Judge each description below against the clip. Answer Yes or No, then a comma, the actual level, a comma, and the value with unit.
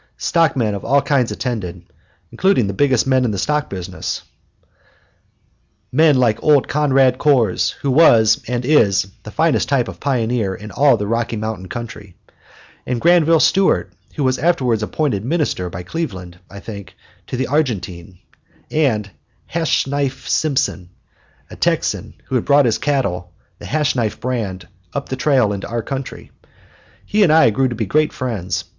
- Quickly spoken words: No, average, 155 wpm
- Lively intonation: Yes, wide, 5.7 semitones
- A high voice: No, low, 125 Hz